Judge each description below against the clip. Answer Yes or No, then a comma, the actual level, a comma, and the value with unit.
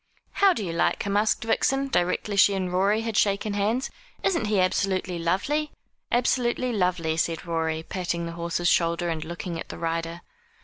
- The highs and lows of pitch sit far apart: No, average, 4.3 semitones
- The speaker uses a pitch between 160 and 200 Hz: Yes, medium, 185 Hz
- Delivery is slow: No, average, 175 wpm